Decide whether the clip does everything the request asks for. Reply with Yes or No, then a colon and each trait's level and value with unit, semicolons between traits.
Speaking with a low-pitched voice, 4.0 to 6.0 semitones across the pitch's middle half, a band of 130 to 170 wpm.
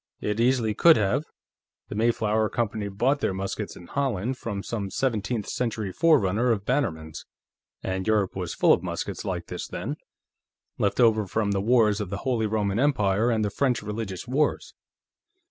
No: low, 110 Hz; average, 3.5 semitones; average, 165 wpm